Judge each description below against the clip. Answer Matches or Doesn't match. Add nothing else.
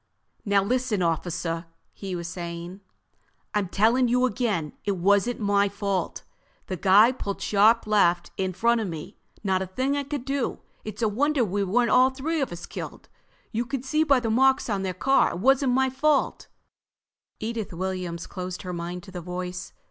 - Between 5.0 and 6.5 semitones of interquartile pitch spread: Matches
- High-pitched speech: Matches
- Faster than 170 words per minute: Matches